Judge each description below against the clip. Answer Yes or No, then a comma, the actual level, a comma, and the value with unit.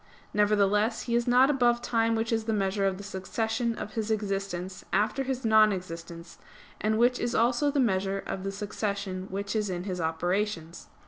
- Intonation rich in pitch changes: No, average, 3.0 semitones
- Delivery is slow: No, average, 185 wpm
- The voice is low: No, high, 210 Hz